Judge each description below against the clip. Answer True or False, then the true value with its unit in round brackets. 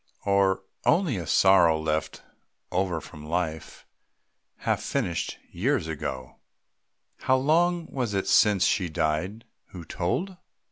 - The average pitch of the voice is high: False (95 Hz)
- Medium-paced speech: False (120 wpm)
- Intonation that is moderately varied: False (6.6 semitones)